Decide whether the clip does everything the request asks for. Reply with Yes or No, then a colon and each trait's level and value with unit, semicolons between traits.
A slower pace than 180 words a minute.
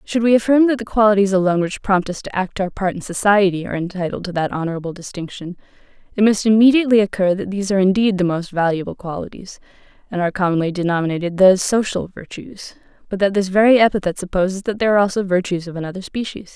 No: average, 200 wpm